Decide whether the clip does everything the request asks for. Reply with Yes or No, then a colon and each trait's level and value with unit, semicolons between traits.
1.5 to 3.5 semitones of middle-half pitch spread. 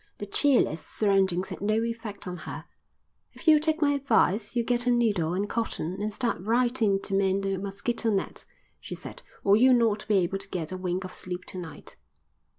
No: average, 3.9 semitones